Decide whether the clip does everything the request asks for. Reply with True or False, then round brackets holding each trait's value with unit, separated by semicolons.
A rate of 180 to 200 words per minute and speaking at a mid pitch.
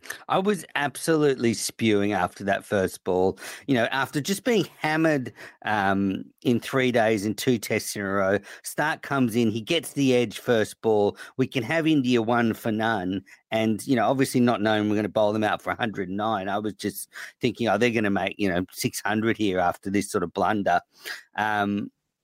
False (195 wpm; 115 Hz)